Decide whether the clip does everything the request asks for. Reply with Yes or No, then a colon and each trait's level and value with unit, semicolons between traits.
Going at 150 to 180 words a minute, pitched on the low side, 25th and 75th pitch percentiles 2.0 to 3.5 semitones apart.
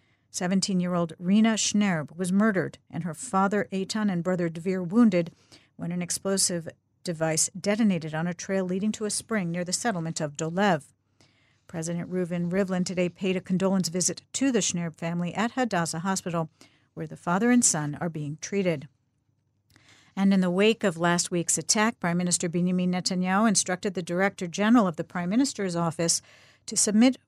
No: average, 170 wpm; medium, 180 Hz; average, 3.1 semitones